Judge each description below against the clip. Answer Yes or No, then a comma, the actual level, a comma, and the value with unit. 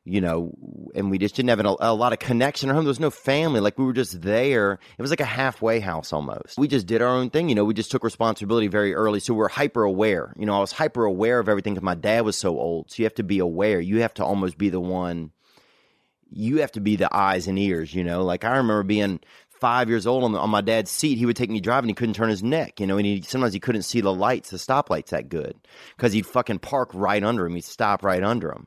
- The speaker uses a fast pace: Yes, fast, 280 wpm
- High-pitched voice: No, low, 110 Hz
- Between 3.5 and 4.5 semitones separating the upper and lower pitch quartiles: Yes, average, 3.8 semitones